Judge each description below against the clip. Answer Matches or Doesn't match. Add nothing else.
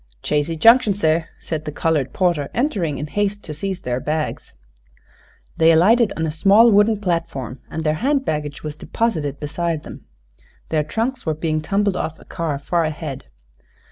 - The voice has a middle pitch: Matches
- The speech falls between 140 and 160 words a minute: Doesn't match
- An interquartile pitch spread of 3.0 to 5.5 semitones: Matches